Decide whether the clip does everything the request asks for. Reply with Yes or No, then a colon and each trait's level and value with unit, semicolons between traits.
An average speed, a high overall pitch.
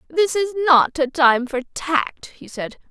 Yes: average, 185 wpm; very high, 300 Hz